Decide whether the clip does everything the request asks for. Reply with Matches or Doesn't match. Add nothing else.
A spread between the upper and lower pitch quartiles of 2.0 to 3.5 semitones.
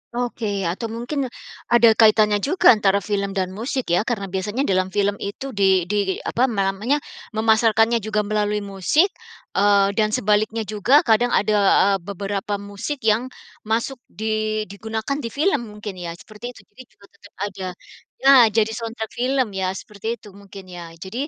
Matches